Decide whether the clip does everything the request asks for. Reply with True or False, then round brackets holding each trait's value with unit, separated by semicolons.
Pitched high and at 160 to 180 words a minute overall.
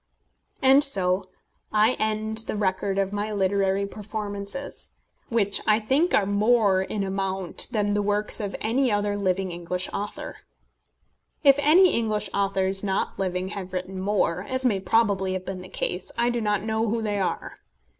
True (205 Hz; 165 wpm)